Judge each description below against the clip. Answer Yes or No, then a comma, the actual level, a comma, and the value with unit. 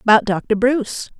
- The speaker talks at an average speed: Yes, average, 150 wpm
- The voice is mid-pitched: No, high, 225 Hz